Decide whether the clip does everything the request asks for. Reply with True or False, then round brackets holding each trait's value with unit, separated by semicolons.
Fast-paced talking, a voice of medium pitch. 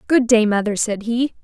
False (210 wpm; 230 Hz)